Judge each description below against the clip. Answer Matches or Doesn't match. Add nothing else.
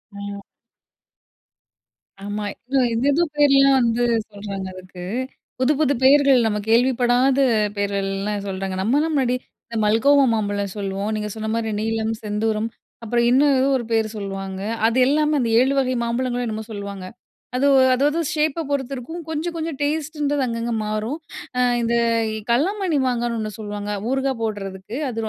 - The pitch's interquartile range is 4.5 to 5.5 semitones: Matches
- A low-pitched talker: Doesn't match